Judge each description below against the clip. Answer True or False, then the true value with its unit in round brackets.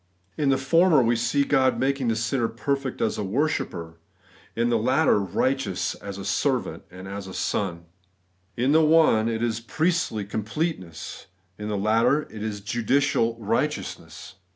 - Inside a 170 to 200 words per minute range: False (150 wpm)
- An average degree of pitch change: True (4.9 semitones)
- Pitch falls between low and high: False (115 Hz)